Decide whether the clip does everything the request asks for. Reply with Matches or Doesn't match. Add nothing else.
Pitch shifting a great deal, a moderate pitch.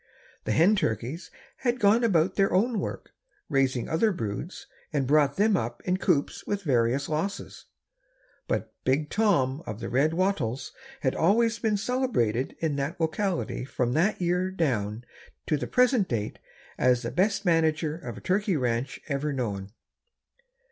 Matches